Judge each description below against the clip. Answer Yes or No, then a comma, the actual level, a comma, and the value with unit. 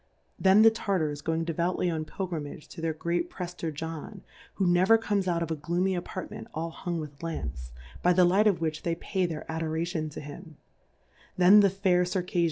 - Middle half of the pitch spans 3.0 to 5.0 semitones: No, narrow, 2.5 semitones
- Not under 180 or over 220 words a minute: Yes, average, 200 wpm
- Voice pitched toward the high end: No, medium, 170 Hz